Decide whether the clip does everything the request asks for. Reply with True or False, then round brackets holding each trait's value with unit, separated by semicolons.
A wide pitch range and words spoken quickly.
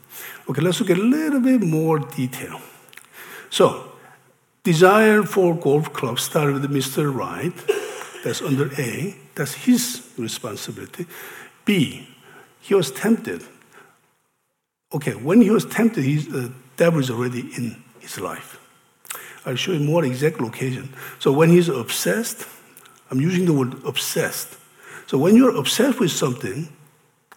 False (7.2 semitones; 150 wpm)